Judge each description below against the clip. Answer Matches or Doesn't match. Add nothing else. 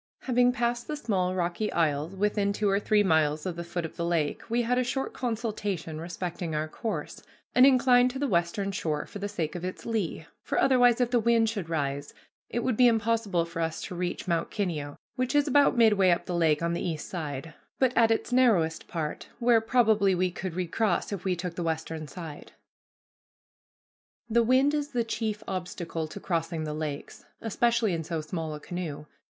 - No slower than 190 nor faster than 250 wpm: Matches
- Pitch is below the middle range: Doesn't match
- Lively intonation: Matches